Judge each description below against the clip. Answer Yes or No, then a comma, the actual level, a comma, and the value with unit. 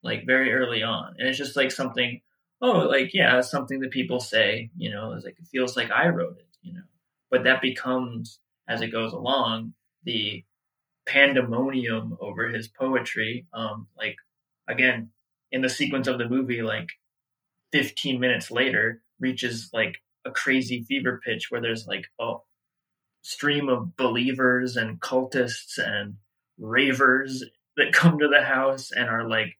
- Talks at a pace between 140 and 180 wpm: Yes, average, 160 wpm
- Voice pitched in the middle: No, low, 125 Hz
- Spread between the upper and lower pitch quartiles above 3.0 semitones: No, average, 2.7 semitones